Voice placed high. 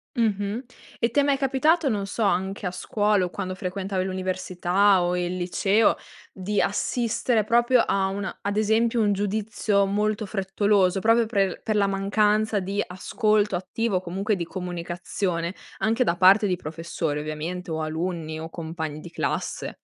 Yes: high, 195 Hz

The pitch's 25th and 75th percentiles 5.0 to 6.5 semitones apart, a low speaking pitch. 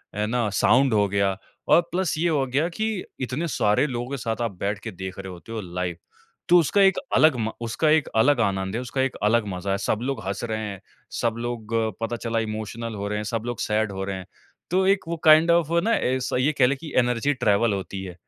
Yes: average, 5.3 semitones; low, 115 Hz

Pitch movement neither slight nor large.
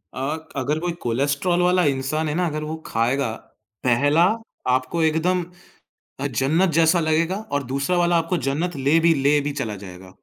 Yes: average, 3.8 semitones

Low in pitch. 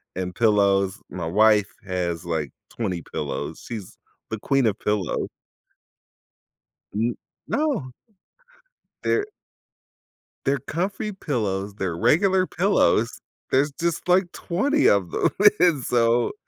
Yes: low, 115 Hz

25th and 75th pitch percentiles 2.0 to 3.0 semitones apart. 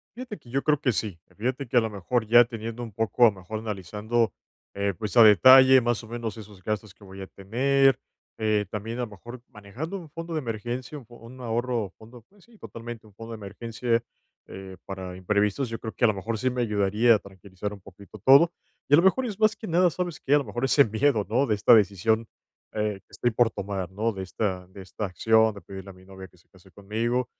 No: average, 3.8 semitones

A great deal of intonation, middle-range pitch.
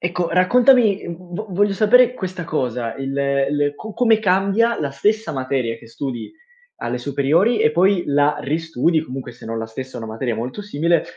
Yes: wide, 7.2 semitones; medium, 165 Hz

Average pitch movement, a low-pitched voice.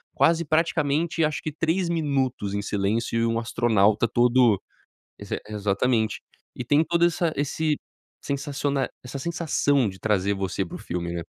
No: wide, 6.5 semitones; low, 130 Hz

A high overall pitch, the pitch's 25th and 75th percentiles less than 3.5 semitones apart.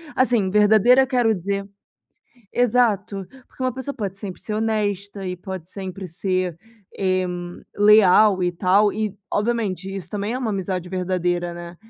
Yes: high, 200 Hz; average, 2.7 semitones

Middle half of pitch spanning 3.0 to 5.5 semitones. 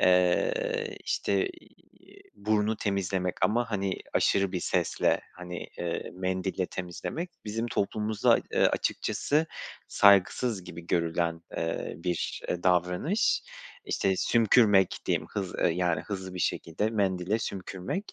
Yes: average, 3.4 semitones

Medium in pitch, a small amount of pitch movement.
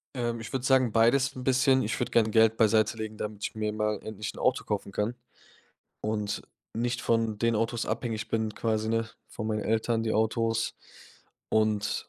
No: low, 110 Hz; narrow, 1.5 semitones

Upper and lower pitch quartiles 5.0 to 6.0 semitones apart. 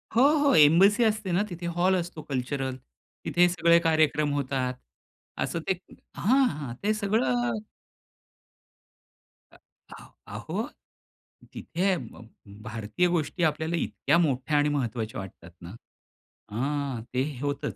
Yes: wide, 5.5 semitones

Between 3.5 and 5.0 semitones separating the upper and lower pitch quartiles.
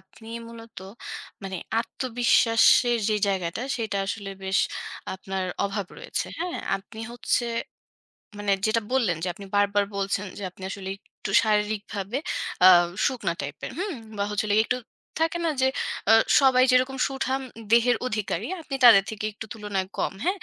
Yes: average, 4.0 semitones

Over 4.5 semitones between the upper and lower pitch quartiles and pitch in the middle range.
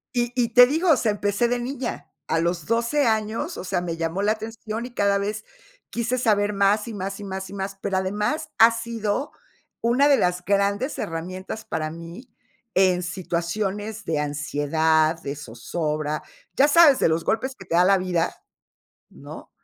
No: average, 5.1 semitones; high, 200 Hz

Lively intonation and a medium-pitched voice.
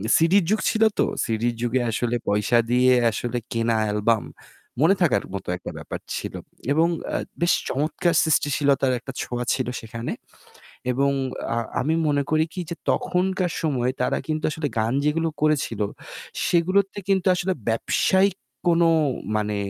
Yes: wide, 6.2 semitones; medium, 145 Hz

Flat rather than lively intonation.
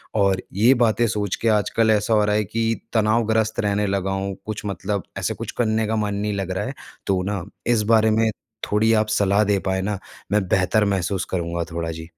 Yes: narrow, 2.1 semitones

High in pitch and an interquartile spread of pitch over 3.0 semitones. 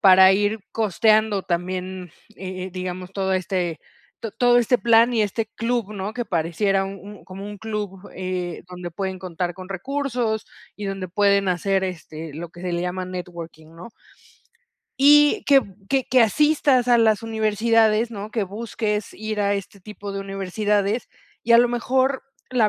Yes: high, 200 Hz; average, 3.4 semitones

